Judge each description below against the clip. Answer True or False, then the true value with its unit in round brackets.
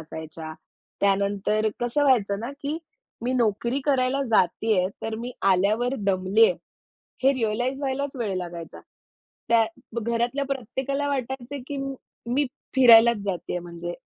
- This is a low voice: False (230 Hz)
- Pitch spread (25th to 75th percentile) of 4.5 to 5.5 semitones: True (4.9 semitones)